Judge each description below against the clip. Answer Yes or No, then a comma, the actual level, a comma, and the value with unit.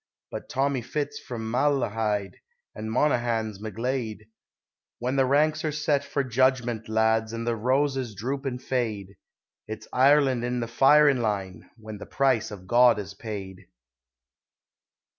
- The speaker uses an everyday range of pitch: Yes, average, 3.5 semitones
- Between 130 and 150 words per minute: Yes, average, 140 wpm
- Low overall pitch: Yes, low, 120 Hz